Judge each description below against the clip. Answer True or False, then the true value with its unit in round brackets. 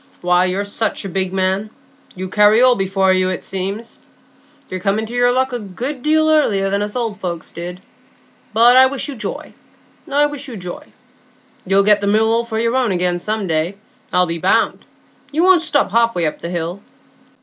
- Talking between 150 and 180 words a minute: False (200 wpm)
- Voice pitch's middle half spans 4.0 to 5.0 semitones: True (4.7 semitones)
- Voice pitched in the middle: False (205 Hz)